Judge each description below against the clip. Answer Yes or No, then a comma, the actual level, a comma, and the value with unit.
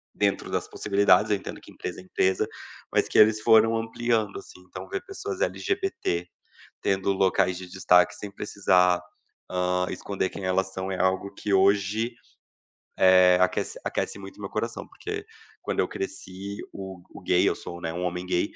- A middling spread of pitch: No, narrow, 2.3 semitones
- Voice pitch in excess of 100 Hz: No, very low, 95 Hz